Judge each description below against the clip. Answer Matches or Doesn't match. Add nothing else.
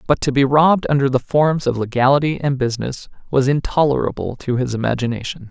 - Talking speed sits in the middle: Matches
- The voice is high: Doesn't match